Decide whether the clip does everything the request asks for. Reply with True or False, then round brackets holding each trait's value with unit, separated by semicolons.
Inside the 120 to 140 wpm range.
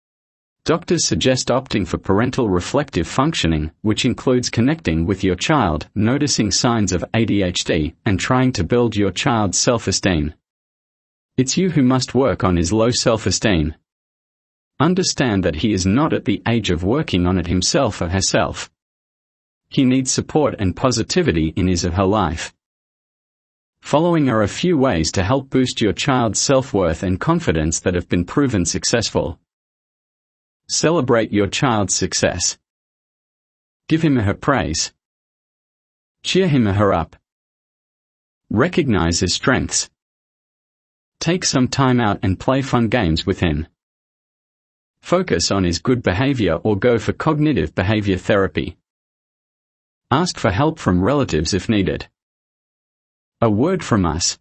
True (135 wpm)